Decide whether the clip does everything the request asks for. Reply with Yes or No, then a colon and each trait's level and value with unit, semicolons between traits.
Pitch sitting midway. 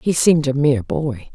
Yes: medium, 150 Hz